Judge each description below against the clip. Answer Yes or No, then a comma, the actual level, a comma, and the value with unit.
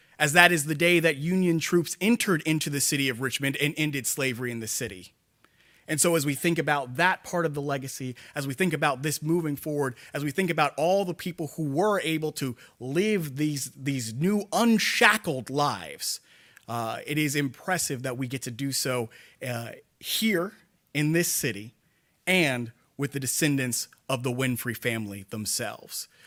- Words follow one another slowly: No, average, 180 wpm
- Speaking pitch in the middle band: Yes, medium, 145 Hz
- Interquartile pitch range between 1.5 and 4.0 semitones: No, average, 4.4 semitones